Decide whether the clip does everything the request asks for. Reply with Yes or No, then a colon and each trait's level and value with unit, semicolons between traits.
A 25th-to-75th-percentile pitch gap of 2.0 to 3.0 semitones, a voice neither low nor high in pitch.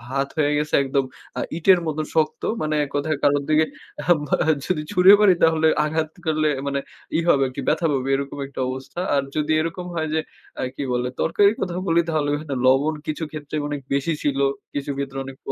Yes: narrow, 2.5 semitones; medium, 150 Hz